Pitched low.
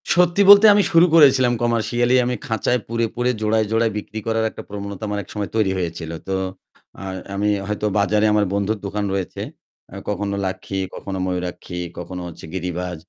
Yes: low, 105 Hz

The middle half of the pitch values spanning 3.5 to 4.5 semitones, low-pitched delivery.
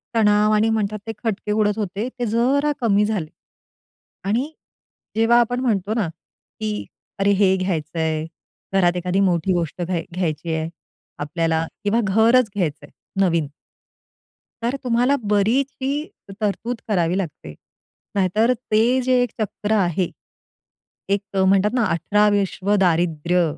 No: average, 4.0 semitones; high, 200 Hz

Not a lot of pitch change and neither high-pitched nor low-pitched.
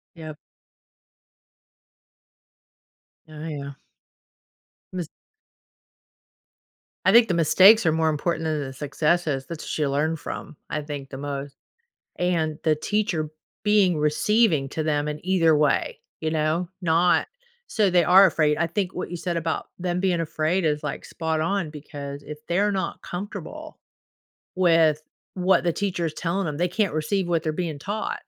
No: average, 3.0 semitones; medium, 160 Hz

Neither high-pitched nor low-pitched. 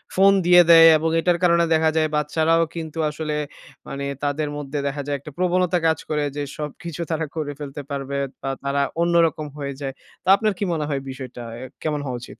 Yes: medium, 155 Hz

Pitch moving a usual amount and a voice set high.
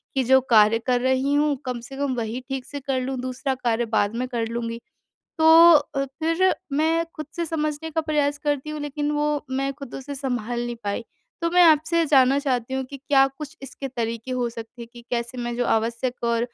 Yes: average, 3.5 semitones; very high, 265 Hz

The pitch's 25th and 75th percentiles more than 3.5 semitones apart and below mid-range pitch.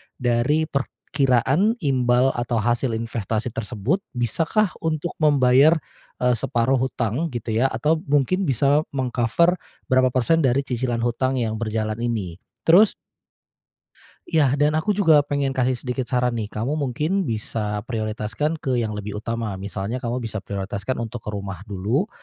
Yes: average, 4.3 semitones; low, 125 Hz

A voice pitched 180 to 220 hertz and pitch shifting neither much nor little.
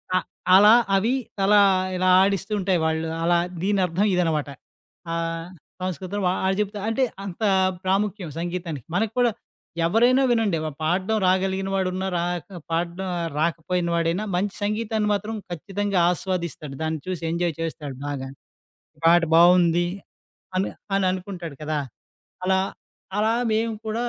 Yes: medium, 185 Hz; average, 3.2 semitones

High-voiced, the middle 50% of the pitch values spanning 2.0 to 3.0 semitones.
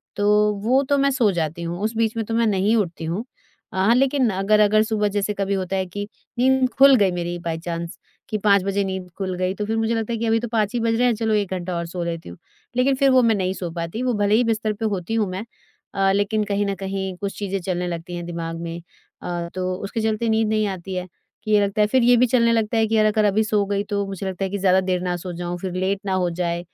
No: high, 200 Hz; average, 3.4 semitones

